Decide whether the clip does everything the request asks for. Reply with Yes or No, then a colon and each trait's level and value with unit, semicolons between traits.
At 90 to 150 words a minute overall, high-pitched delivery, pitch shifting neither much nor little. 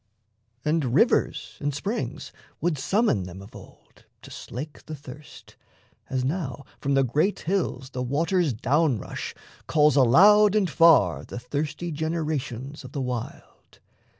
No: average, 140 wpm; medium, 145 Hz; average, 4.4 semitones